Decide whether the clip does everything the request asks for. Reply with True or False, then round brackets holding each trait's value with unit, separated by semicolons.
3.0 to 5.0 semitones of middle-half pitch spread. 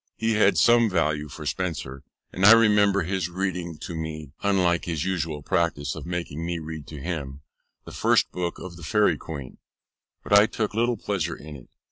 True (4.1 semitones)